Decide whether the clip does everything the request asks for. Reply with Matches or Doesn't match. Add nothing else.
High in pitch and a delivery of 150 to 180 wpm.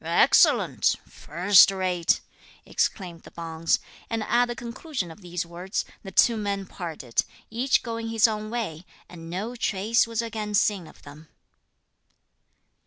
Doesn't match